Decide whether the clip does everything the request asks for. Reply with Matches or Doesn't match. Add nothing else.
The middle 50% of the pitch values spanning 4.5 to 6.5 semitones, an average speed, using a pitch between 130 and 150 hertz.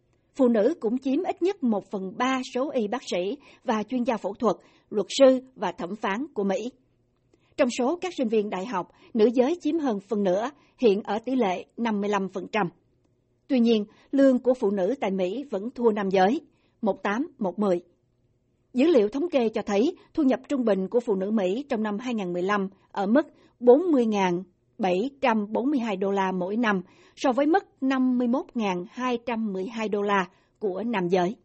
Doesn't match